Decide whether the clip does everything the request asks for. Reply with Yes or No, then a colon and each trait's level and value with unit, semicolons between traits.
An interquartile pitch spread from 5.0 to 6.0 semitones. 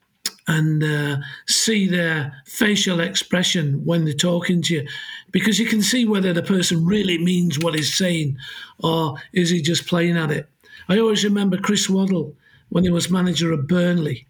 No: average, 3.0 semitones